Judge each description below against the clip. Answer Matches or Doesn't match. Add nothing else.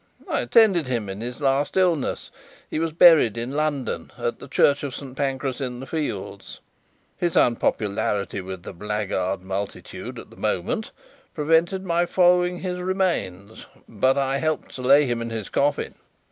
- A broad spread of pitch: Matches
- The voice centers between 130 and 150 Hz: Matches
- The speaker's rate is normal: Matches